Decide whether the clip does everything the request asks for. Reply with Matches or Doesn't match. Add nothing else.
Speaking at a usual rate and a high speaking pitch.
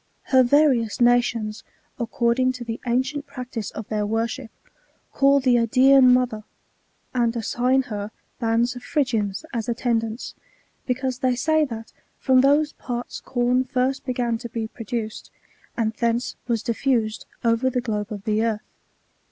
Matches